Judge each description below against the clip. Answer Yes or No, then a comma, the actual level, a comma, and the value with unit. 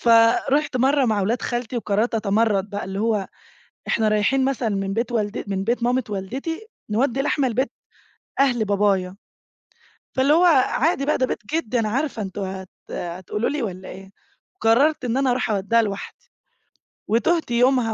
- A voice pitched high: Yes, high, 230 Hz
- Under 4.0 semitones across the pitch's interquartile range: No, average, 4.3 semitones